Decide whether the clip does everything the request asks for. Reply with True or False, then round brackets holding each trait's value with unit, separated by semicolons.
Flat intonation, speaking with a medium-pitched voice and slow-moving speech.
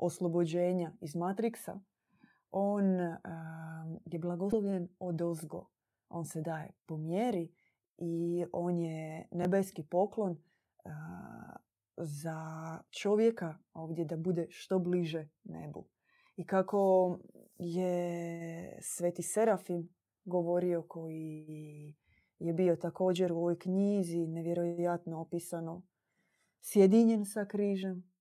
True (2.0 semitones; 175 Hz; 100 wpm)